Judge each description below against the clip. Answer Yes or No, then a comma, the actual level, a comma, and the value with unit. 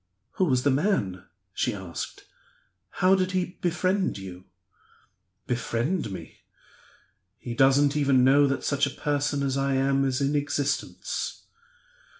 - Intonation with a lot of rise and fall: No, narrow, 2.5 semitones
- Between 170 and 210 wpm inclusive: No, slow, 135 wpm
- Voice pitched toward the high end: No, medium, 140 Hz